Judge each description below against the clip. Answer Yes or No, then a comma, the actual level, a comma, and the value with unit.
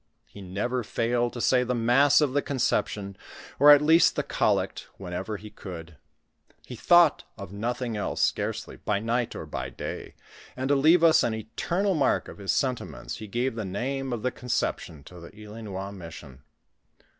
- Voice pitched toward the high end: No, low, 115 Hz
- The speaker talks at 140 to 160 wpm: No, average, 175 wpm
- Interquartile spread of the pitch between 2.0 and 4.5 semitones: No, average, 5.1 semitones